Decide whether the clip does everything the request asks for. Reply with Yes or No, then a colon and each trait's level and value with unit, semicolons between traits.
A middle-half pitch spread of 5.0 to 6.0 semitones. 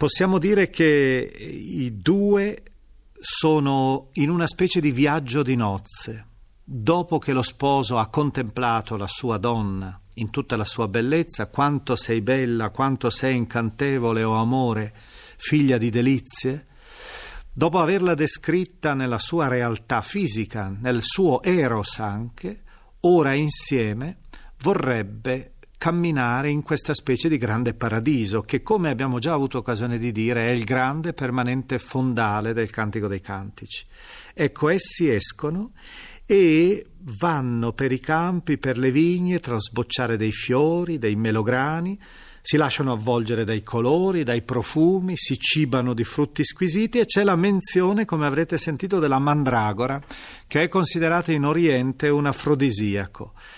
Yes: wide, 5.5 semitones